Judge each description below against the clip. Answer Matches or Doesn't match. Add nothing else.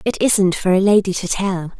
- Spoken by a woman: Matches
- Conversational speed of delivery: Doesn't match